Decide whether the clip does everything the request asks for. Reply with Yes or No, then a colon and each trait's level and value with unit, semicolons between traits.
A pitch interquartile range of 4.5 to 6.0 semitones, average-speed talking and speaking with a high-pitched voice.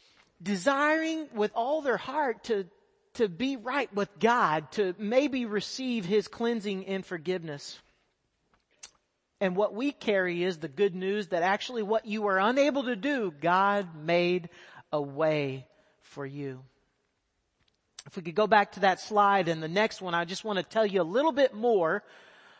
Yes: average, 5.2 semitones; average, 165 wpm; high, 200 Hz